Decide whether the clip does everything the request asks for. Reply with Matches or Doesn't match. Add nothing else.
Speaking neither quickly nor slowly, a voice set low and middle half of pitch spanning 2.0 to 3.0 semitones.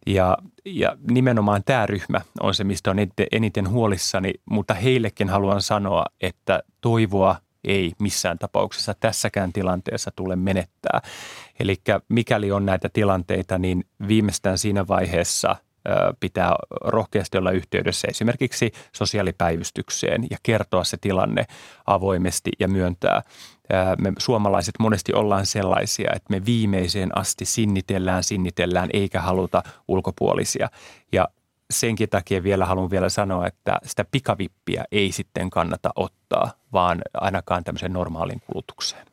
Matches